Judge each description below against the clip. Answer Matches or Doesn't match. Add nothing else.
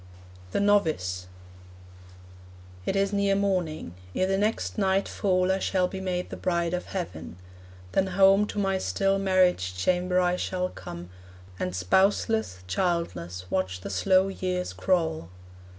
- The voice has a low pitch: Doesn't match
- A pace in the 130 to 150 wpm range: Matches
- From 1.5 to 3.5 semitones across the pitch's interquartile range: Doesn't match